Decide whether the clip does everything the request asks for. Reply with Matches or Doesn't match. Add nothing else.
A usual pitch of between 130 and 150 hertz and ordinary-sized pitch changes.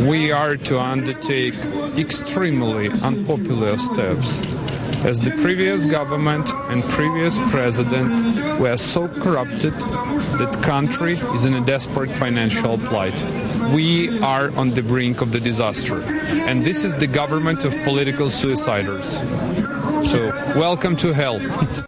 Matches